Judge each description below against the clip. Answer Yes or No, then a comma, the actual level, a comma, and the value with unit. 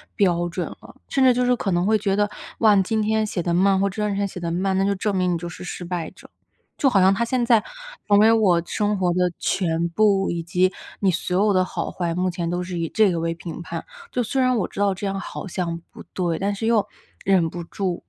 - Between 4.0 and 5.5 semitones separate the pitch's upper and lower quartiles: No, average, 3.1 semitones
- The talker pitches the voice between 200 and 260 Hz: No, high, 190 Hz